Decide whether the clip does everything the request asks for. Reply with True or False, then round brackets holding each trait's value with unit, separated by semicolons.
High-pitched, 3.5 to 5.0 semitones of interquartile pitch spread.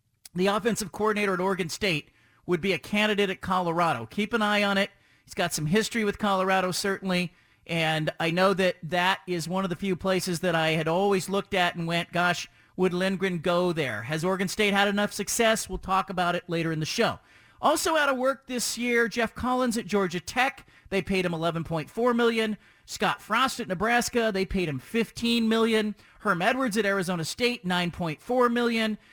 True (195 Hz; 3.9 semitones)